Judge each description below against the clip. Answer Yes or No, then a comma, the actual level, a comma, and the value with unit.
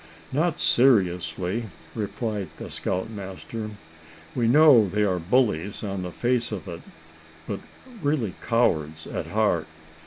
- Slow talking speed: Yes, slow, 120 wpm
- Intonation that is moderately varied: Yes, average, 4.8 semitones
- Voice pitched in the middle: No, low, 105 Hz